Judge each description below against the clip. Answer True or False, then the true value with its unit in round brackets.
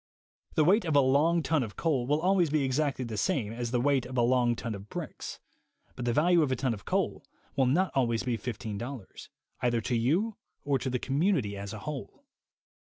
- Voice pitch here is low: True (130 Hz)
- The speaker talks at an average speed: False (215 wpm)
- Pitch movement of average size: True (4.4 semitones)